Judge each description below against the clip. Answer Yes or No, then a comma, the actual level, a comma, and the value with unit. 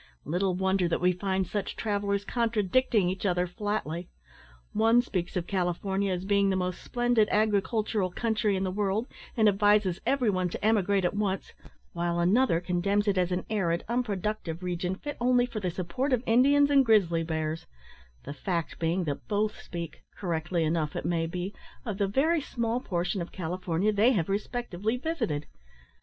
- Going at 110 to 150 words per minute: No, average, 170 wpm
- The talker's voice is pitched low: No, high, 195 Hz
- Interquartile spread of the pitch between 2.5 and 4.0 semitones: Yes, average, 3.6 semitones